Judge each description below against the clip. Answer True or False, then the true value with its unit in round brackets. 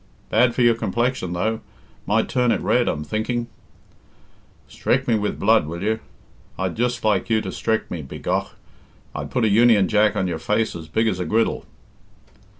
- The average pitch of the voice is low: True (110 Hz)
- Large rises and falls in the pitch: False (3.8 semitones)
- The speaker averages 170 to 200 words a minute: True (180 wpm)